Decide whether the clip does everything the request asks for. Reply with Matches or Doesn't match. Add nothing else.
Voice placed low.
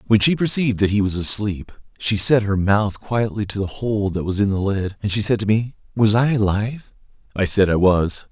Matches